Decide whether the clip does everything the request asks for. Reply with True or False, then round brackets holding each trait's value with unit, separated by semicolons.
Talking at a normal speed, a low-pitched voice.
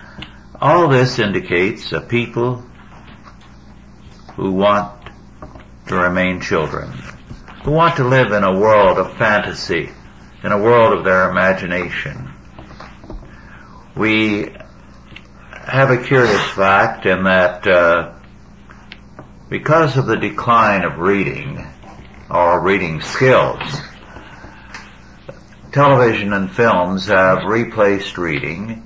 False (100 wpm; 105 Hz)